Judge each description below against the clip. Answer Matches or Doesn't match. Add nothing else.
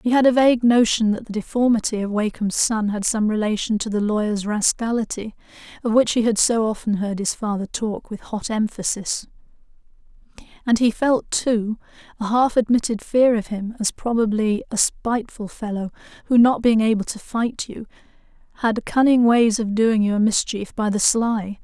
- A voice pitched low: Doesn't match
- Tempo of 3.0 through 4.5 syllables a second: Doesn't match